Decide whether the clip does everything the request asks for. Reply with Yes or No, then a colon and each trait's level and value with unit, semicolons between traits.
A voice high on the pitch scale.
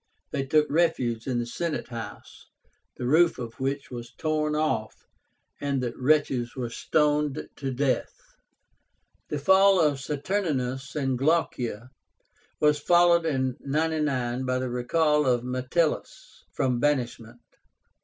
No: low, 135 Hz